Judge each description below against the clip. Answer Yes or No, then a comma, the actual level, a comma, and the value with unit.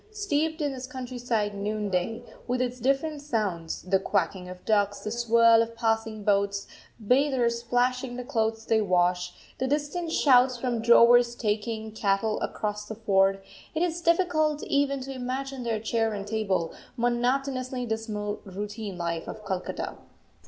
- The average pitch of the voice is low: No, high, 230 Hz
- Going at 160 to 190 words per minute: No, average, 145 wpm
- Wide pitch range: No, average, 3.7 semitones